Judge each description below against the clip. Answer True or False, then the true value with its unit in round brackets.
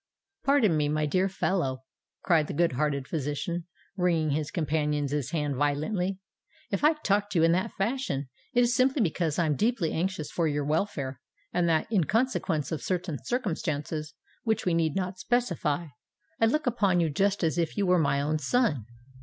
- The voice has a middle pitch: True (170 Hz)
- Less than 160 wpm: False (175 wpm)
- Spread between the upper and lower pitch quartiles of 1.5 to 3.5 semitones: False (4.9 semitones)